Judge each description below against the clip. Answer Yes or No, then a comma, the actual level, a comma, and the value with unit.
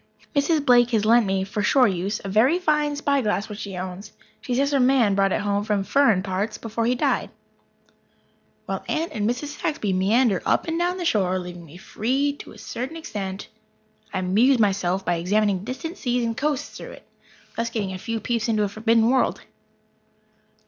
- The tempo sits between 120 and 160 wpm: No, average, 190 wpm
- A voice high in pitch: Yes, high, 225 Hz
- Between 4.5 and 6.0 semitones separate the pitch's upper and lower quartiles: Yes, average, 5.1 semitones